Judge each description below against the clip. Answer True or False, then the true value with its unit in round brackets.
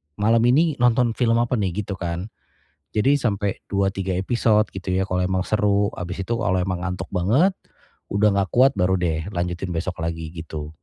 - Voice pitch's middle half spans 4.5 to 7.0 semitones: False (3.8 semitones)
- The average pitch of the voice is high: False (95 Hz)